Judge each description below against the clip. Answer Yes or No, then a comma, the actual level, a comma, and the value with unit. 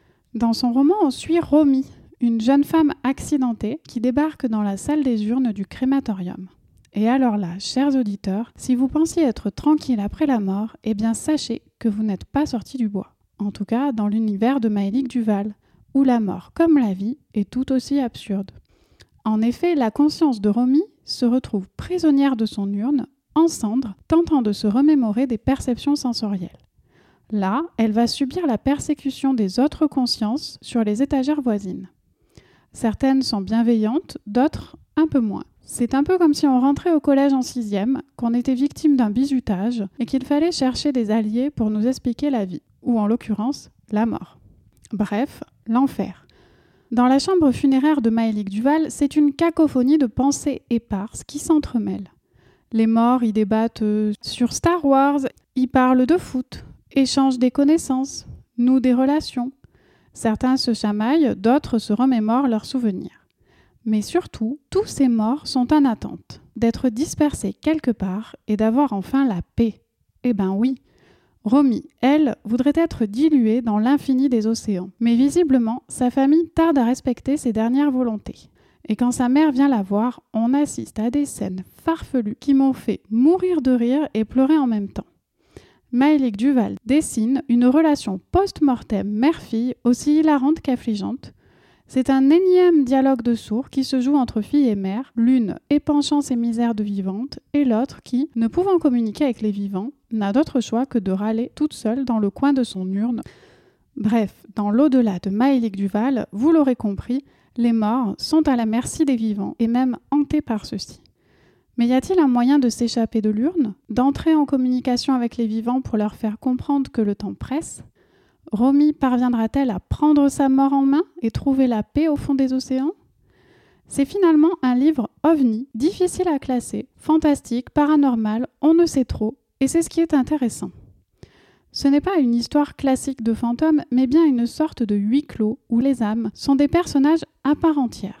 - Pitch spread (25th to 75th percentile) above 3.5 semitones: Yes, average, 4.1 semitones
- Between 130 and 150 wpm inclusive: No, average, 170 wpm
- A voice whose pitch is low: No, very high, 255 Hz